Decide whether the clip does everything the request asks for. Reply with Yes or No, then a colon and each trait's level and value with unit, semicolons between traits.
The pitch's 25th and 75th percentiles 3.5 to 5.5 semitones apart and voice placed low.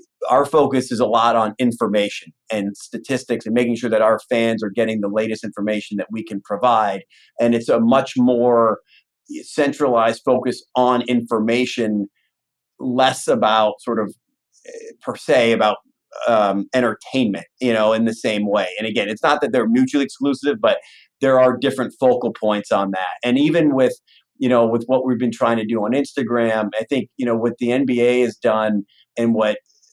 No: average, 2.9 semitones; low, 120 Hz